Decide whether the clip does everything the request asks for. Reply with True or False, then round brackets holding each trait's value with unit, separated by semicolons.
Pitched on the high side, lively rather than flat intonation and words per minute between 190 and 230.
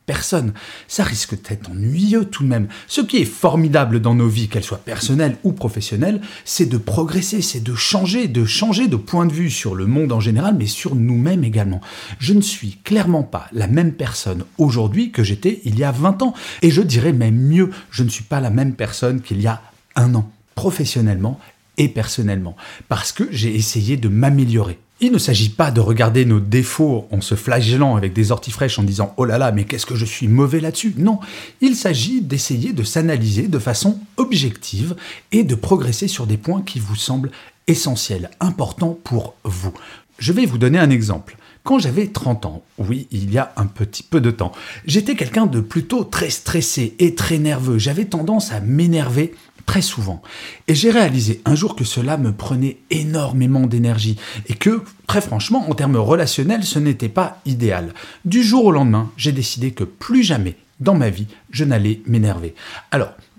False (125 Hz; 7.2 semitones; 195 wpm)